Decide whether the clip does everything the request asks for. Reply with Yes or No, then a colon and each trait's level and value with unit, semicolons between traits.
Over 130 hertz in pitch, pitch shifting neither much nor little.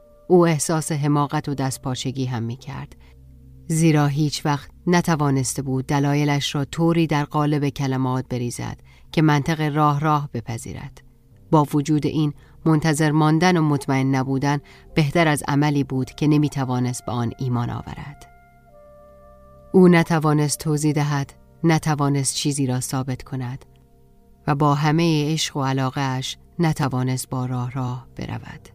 Yes: medium, 140 Hz; average, 3.1 semitones